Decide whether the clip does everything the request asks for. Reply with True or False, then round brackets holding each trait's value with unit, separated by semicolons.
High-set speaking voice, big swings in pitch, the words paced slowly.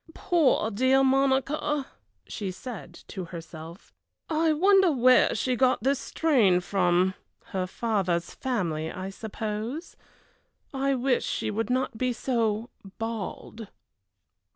True (230 Hz; 5.8 semitones; 115 wpm)